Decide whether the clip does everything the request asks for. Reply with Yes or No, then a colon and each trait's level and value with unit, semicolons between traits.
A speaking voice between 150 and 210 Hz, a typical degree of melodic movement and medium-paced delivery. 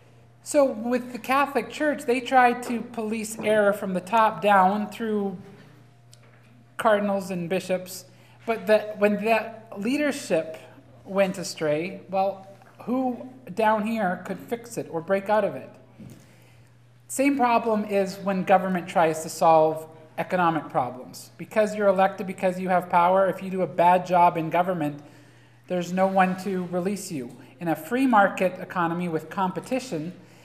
Yes: high, 190 Hz; average, 4.7 semitones; average, 150 wpm